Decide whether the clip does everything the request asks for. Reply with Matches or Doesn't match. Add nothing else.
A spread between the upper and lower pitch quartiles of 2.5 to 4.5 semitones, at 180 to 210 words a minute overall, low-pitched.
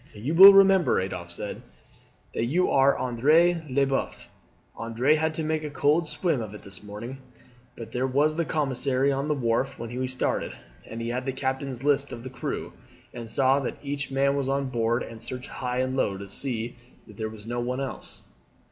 Matches